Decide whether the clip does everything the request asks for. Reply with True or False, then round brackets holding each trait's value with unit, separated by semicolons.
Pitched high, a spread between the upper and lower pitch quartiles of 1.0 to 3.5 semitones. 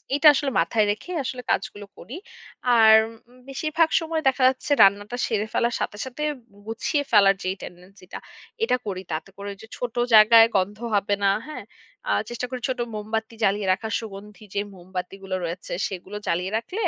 False (215 Hz; 4.2 semitones)